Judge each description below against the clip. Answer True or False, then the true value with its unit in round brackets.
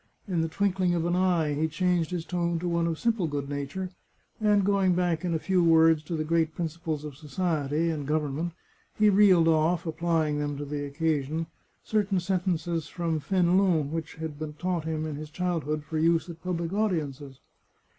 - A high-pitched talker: False (165 Hz)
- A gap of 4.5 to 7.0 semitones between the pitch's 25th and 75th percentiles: False (2.7 semitones)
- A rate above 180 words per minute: True (190 wpm)